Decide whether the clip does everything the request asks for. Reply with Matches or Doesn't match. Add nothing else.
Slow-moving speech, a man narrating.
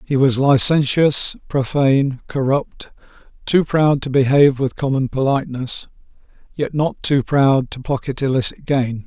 Matches